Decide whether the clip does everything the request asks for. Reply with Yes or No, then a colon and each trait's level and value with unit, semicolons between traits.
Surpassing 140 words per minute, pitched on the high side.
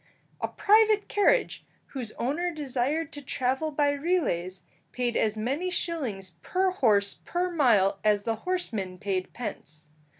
No: slow, 135 wpm; very high, 265 Hz